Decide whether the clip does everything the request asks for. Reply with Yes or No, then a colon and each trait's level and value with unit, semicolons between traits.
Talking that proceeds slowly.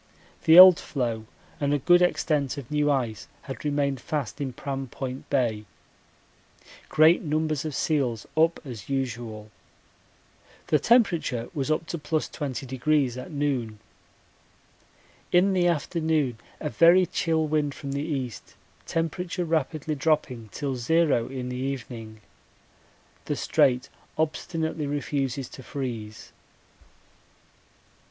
Yes: slow, 120 wpm